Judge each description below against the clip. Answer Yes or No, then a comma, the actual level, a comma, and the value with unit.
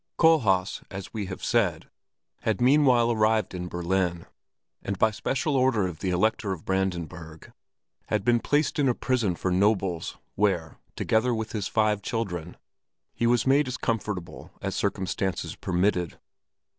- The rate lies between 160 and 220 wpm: No, average, 145 wpm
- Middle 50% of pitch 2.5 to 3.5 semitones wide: No, average, 4.5 semitones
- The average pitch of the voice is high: No, low, 105 Hz